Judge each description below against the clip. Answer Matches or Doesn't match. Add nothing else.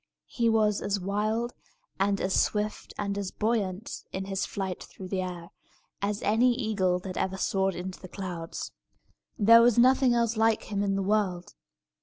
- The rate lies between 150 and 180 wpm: Matches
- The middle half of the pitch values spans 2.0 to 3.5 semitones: Matches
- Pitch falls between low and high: Doesn't match